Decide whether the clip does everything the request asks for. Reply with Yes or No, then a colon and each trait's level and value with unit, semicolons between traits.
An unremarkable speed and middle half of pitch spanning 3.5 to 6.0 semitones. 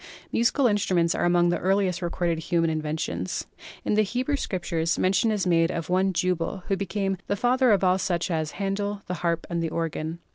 No: average, 190 wpm; average, 3.0 semitones